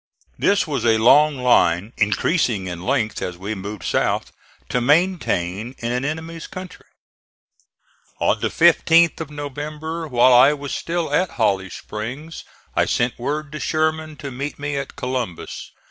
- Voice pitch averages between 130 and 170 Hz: Yes, medium, 140 Hz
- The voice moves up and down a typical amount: No, wide, 5.7 semitones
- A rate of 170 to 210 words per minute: No, average, 150 wpm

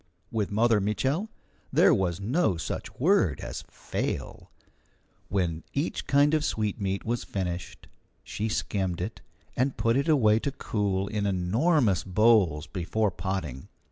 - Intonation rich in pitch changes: No, average, 4.6 semitones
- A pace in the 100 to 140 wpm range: Yes, slow, 135 wpm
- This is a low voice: Yes, low, 105 Hz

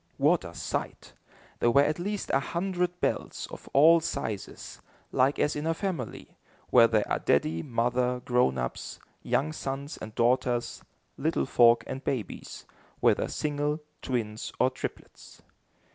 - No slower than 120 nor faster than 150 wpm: Yes, average, 145 wpm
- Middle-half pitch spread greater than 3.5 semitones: Yes, average, 4.5 semitones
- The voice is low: Yes, low, 130 Hz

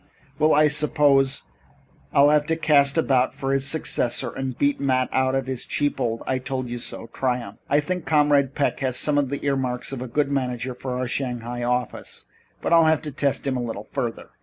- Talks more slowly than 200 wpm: No, fast, 205 wpm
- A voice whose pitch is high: No, low, 135 Hz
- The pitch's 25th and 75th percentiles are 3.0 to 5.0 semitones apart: No, narrow, 2.5 semitones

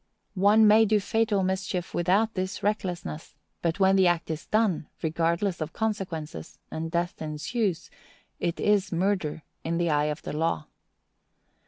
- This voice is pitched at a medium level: Yes, medium, 180 Hz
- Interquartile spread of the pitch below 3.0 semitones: No, average, 3.8 semitones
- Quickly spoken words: No, average, 150 wpm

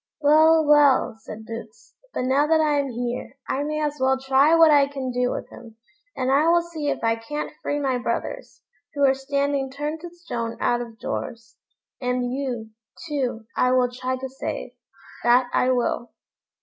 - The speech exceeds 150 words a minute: Yes, average, 185 wpm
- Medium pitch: No, very high, 265 Hz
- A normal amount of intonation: Yes, average, 3.2 semitones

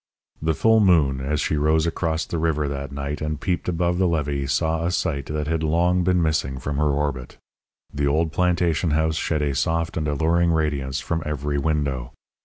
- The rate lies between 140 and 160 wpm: No, average, 195 wpm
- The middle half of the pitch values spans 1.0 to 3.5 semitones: Yes, narrow, 2.6 semitones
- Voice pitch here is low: Yes, very low, 75 Hz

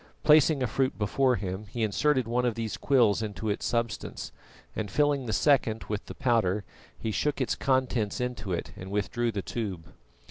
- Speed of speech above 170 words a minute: Yes, average, 180 wpm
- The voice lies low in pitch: Yes, low, 115 Hz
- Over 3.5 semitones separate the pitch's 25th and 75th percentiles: Yes, average, 3.9 semitones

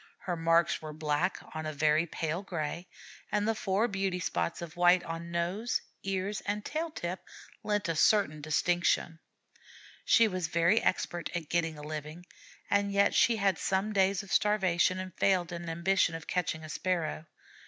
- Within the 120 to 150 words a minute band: No, average, 175 wpm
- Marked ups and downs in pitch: No, average, 3.1 semitones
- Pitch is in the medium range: Yes, medium, 175 Hz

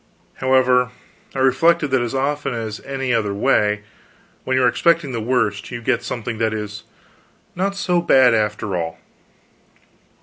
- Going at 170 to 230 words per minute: No, average, 155 wpm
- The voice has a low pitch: Yes, low, 125 Hz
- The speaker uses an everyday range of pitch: Yes, average, 3.8 semitones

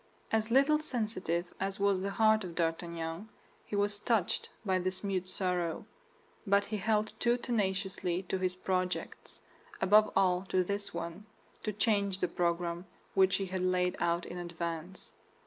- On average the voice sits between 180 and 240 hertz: Yes, high, 190 Hz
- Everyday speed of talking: Yes, average, 155 wpm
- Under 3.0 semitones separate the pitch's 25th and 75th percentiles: Yes, narrow, 2.5 semitones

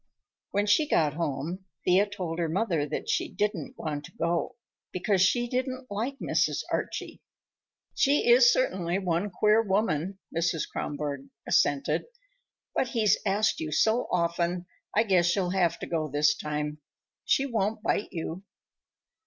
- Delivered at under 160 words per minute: Yes, average, 145 wpm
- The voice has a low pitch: No, medium, 185 Hz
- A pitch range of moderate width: Yes, average, 4.8 semitones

